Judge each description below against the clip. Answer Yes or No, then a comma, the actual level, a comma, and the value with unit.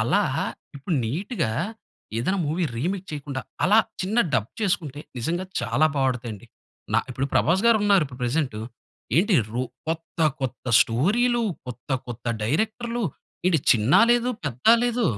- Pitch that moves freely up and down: Yes, wide, 8.3 semitones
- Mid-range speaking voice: Yes, medium, 160 Hz